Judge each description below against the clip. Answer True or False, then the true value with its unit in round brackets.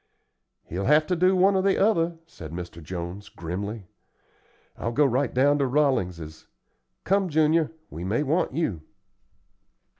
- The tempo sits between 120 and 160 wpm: True (145 wpm)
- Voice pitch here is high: False (135 Hz)